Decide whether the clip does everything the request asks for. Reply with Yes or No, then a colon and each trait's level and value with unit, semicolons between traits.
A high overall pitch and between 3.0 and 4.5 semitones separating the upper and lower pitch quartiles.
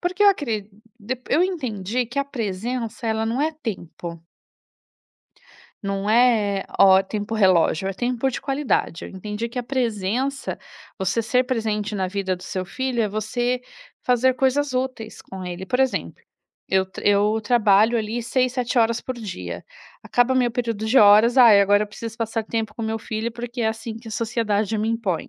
Yes: high, 225 Hz; average, 3.3 semitones